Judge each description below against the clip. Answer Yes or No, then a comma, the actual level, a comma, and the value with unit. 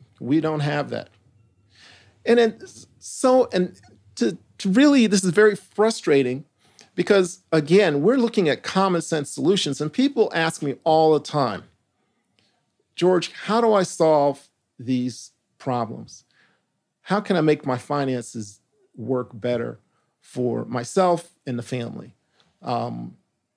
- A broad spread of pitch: Yes, wide, 7.7 semitones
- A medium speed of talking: No, slow, 130 wpm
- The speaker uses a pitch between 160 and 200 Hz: No, medium, 150 Hz